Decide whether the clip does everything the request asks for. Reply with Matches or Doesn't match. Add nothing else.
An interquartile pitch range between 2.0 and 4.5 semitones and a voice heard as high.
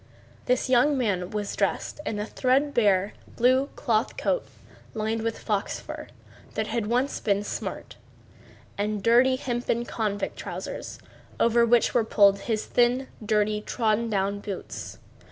Matches